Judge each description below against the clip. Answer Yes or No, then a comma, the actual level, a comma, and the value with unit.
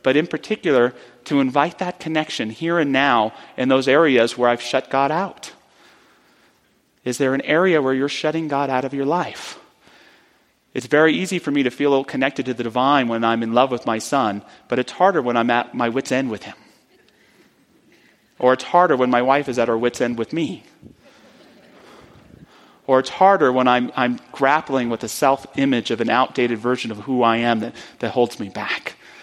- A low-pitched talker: Yes, low, 130 Hz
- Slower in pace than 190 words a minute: No, average, 195 wpm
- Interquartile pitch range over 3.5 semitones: No, average, 2.9 semitones